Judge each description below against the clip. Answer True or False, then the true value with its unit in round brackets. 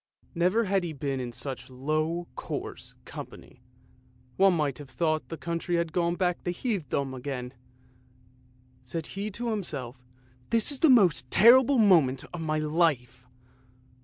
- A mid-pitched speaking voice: True (165 Hz)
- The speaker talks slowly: False (150 wpm)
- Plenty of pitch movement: True (5.8 semitones)